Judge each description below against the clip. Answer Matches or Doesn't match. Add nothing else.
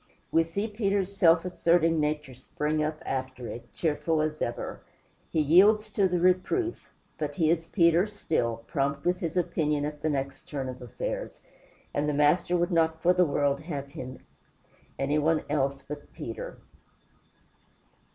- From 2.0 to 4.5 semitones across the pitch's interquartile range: Matches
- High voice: Doesn't match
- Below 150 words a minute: Doesn't match